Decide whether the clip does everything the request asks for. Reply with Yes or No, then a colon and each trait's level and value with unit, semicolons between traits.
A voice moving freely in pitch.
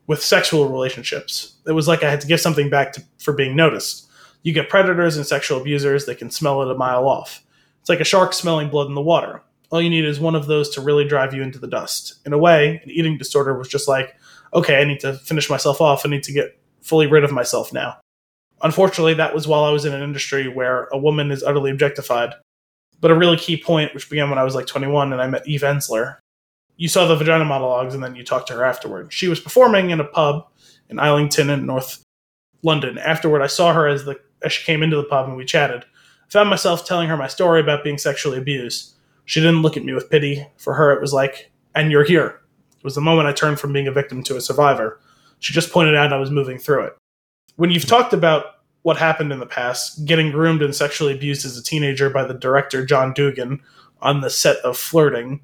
No: average, 2.8 semitones